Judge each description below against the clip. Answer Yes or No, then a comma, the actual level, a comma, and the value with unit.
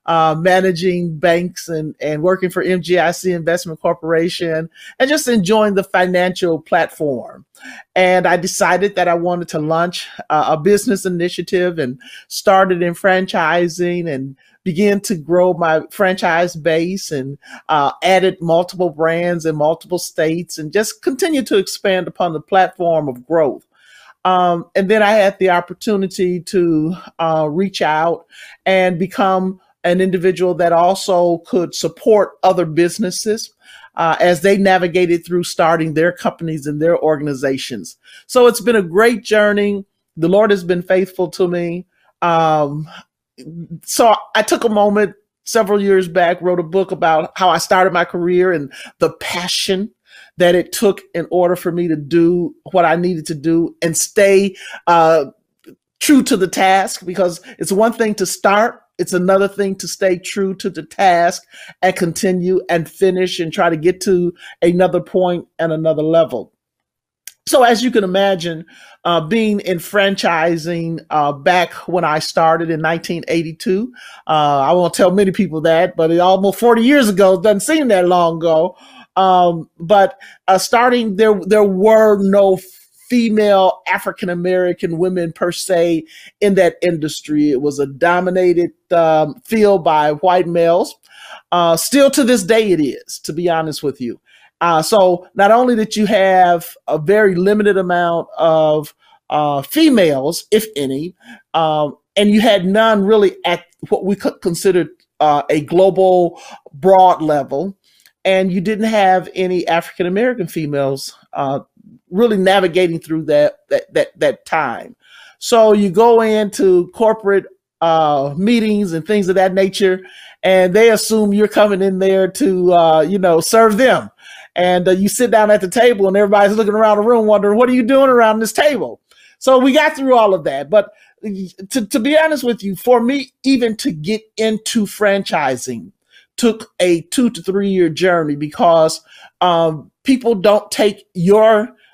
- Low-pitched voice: No, medium, 185 Hz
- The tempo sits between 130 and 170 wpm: Yes, average, 160 wpm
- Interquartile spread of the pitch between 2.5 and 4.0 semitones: Yes, average, 3.4 semitones